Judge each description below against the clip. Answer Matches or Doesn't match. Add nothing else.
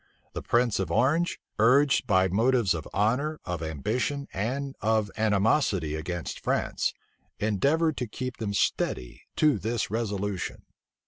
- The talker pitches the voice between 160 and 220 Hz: Doesn't match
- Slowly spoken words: Matches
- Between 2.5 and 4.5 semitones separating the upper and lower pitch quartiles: Doesn't match